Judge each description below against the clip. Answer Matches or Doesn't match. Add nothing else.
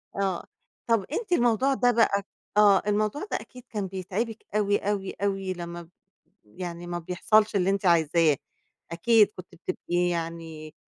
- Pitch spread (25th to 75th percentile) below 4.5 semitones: Matches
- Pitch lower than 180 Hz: Doesn't match